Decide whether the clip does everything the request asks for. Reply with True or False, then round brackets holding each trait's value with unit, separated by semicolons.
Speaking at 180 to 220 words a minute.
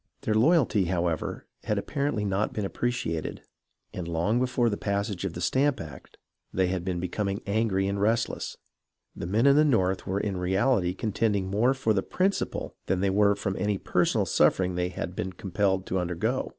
True (190 wpm)